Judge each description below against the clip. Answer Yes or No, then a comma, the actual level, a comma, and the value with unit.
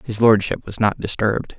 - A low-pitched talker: Yes, low, 105 Hz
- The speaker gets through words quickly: No, average, 190 wpm